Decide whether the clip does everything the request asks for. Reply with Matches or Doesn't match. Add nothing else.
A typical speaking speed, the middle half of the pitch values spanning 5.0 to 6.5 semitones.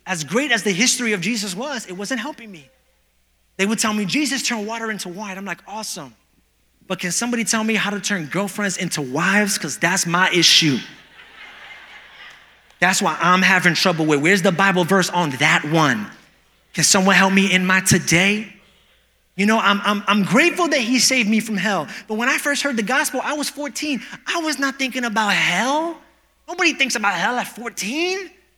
Matches